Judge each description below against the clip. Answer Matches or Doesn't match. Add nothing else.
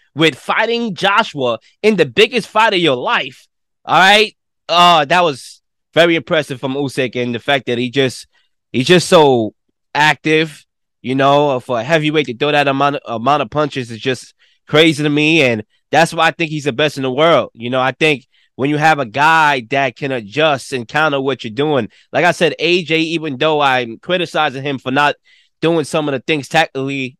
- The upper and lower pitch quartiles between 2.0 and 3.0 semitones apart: Doesn't match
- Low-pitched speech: Doesn't match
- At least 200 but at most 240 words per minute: Matches